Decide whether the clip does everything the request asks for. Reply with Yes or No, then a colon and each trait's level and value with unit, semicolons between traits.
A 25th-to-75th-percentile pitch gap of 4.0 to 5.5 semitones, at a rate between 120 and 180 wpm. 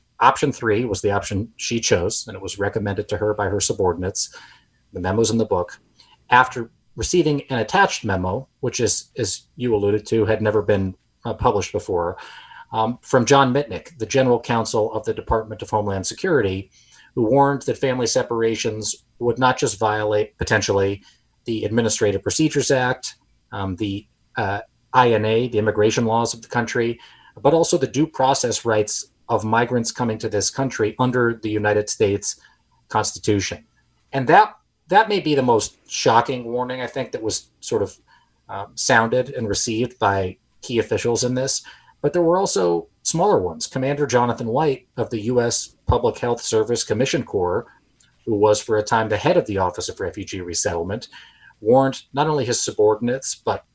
No: average, 3.2 semitones; average, 170 wpm